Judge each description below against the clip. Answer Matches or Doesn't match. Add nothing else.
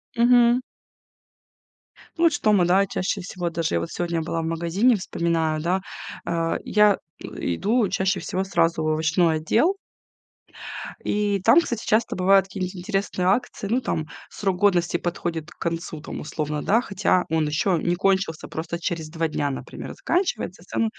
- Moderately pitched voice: Matches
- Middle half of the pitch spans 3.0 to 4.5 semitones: Matches